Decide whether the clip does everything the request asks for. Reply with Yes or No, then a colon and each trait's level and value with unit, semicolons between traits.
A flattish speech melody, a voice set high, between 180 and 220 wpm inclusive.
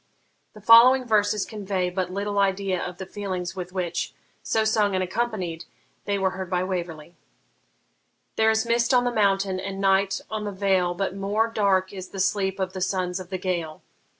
Yes: narrow, 2.1 semitones; high, 195 Hz; average, 185 wpm